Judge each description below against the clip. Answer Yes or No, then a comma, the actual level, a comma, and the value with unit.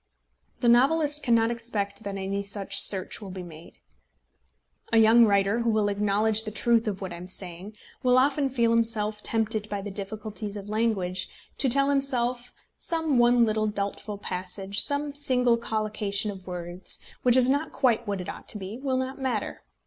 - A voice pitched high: Yes, high, 215 Hz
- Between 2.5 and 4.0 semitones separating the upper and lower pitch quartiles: Yes, average, 3.5 semitones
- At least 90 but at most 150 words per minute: No, average, 180 wpm